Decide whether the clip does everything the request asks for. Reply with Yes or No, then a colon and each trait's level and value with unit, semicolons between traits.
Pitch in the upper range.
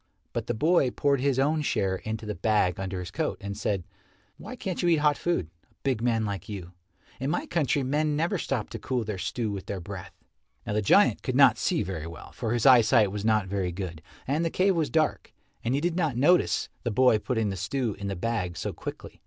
No: low, 115 Hz